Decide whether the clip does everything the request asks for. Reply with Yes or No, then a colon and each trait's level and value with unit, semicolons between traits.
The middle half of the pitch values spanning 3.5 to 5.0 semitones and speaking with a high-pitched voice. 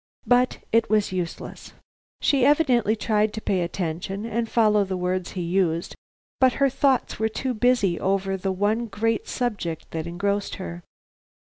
Yes: average, 4.0 semitones; high, 210 Hz